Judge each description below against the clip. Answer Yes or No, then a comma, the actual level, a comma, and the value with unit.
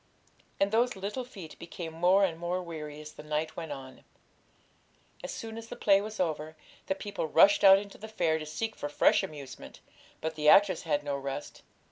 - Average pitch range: Yes, average, 4.7 semitones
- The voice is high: No, medium, 170 Hz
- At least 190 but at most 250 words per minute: Yes, average, 195 wpm